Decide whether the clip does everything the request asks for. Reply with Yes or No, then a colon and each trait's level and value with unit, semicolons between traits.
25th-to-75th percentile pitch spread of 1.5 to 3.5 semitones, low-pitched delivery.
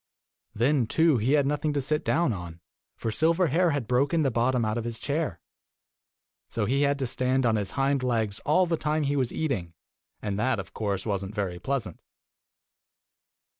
No: average, 5.3 semitones; low, 130 Hz